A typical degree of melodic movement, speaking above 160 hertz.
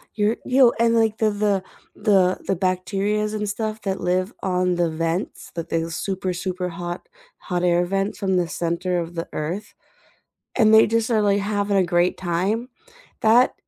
Yes: average, 3.2 semitones; high, 190 Hz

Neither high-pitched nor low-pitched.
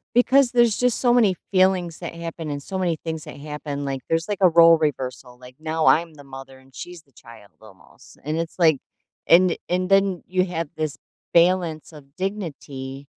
Yes: medium, 165 Hz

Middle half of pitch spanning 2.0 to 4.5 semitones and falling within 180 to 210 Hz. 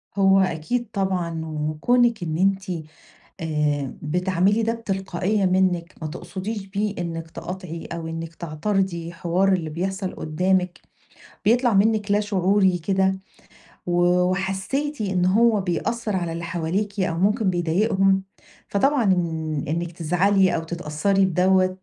Yes: average, 2.9 semitones; medium, 185 Hz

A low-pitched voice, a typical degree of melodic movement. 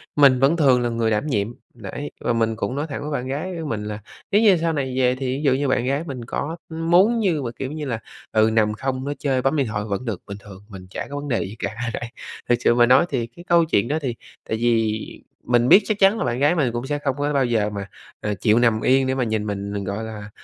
Yes: low, 125 Hz; average, 4.6 semitones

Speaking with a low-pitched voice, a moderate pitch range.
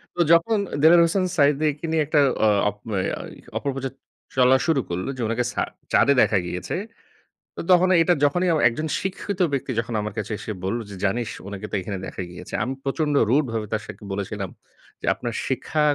No: low, 130 Hz; wide, 6.7 semitones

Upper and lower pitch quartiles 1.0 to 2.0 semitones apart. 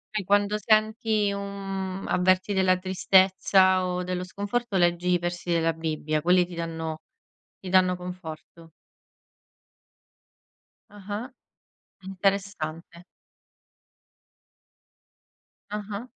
No: narrow, 2.4 semitones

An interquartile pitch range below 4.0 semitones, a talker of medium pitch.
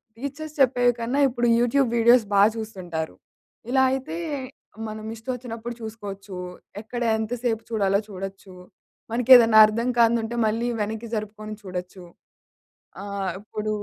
No: average, 2.9 semitones; high, 225 Hz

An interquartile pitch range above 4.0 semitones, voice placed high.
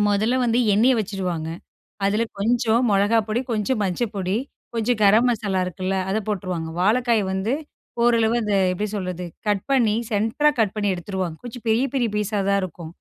No: average, 3.3 semitones; high, 210 Hz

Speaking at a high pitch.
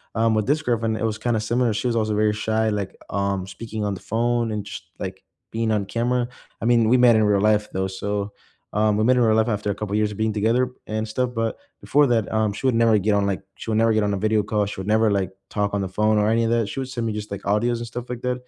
No: low, 110 Hz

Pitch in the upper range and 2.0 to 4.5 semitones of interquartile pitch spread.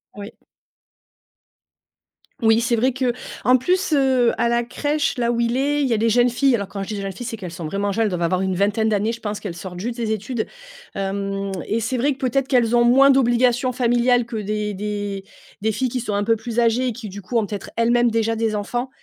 Yes: high, 230 Hz; average, 3.2 semitones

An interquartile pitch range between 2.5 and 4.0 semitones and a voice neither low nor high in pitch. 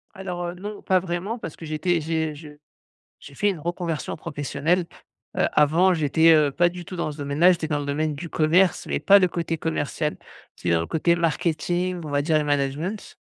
Yes: average, 2.8 semitones; medium, 165 Hz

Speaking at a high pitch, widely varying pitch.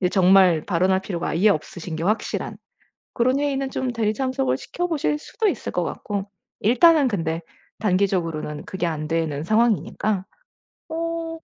Yes: high, 200 Hz; wide, 7.4 semitones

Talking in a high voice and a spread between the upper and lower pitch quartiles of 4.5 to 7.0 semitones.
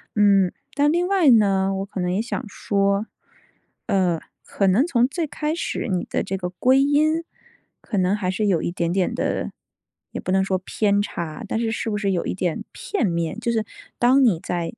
Yes: high, 200 Hz; average, 5.1 semitones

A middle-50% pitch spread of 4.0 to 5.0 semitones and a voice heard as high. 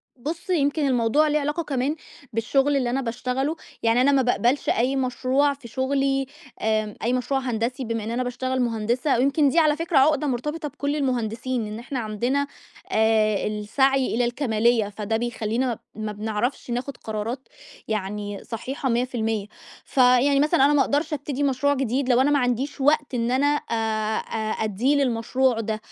No: average, 3.6 semitones; very high, 255 Hz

